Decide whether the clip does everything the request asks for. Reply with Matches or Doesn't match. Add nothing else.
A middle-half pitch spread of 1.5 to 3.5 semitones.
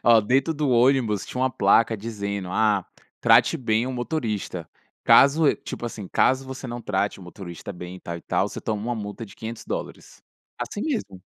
Doesn't match